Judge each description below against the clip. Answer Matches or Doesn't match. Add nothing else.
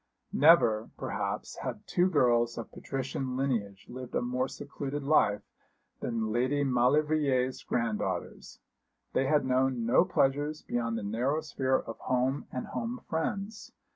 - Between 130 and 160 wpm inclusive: Matches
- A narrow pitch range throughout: Doesn't match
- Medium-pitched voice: Doesn't match